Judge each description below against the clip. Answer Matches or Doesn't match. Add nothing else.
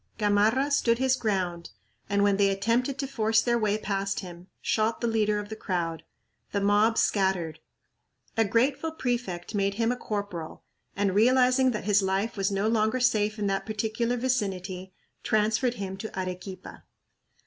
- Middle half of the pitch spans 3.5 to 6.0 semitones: Doesn't match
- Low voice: Doesn't match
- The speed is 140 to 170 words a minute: Matches